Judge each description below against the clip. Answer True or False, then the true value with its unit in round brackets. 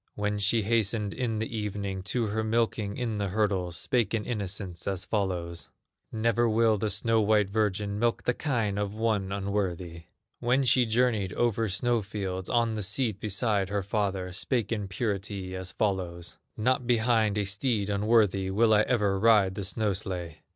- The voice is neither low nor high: False (105 Hz)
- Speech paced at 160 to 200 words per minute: True (170 wpm)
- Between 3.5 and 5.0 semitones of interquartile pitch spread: False (2.7 semitones)